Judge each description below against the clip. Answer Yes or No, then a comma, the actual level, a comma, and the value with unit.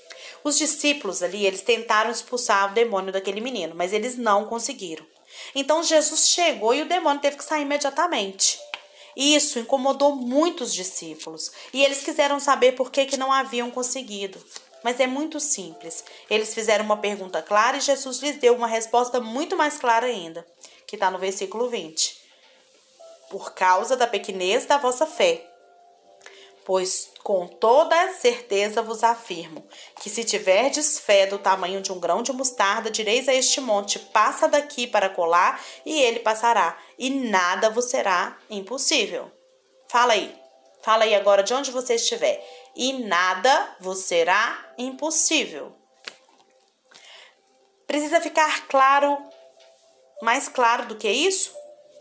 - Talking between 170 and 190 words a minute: No, average, 145 wpm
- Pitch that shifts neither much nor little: No, wide, 6.2 semitones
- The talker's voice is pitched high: Yes, high, 240 Hz